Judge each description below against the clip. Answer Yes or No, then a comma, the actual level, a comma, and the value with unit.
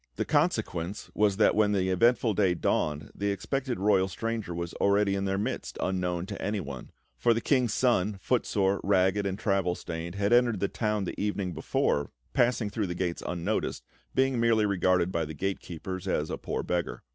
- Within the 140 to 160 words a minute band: No, average, 185 wpm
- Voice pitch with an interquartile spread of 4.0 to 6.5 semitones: No, average, 3.0 semitones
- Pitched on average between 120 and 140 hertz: No, low, 100 Hz